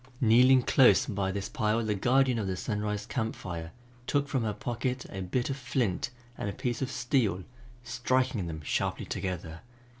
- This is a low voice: Yes, low, 115 Hz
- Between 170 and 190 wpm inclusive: Yes, average, 175 wpm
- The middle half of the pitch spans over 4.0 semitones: Yes, average, 4.8 semitones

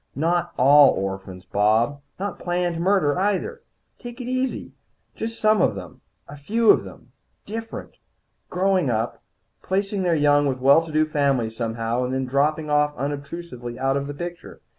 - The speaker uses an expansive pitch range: Yes, wide, 6.2 semitones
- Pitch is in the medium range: Yes, medium, 150 Hz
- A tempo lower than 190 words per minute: Yes, average, 160 wpm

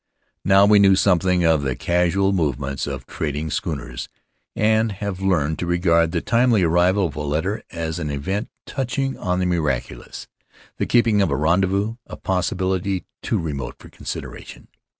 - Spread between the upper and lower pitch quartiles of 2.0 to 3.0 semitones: No, average, 3.7 semitones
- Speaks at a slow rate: No, average, 170 wpm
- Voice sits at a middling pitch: No, very low, 90 Hz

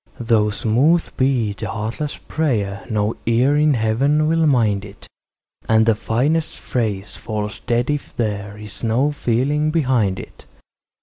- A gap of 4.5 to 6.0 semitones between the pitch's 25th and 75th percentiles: Yes, average, 5.2 semitones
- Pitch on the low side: Yes, low, 115 Hz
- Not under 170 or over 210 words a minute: No, average, 140 wpm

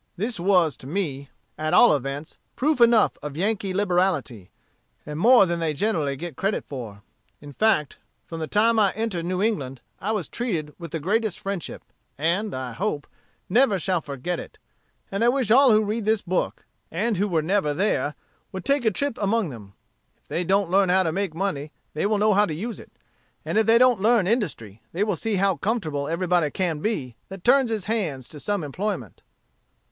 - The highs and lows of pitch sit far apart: Yes, wide, 5.8 semitones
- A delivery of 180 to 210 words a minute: Yes, average, 195 wpm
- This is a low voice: No, medium, 185 Hz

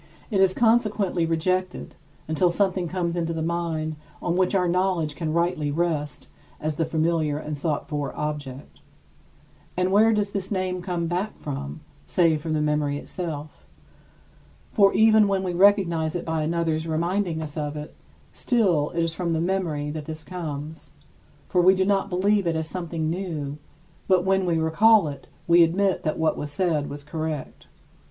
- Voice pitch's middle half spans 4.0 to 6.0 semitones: No, average, 3.1 semitones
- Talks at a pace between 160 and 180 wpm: Yes, average, 170 wpm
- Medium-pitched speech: Yes, medium, 170 Hz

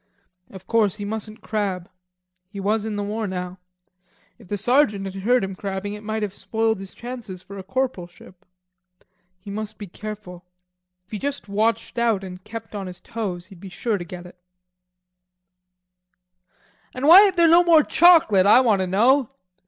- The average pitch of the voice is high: Yes, high, 210 Hz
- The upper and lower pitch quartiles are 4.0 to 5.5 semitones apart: No, average, 3.3 semitones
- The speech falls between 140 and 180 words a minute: Yes, average, 175 wpm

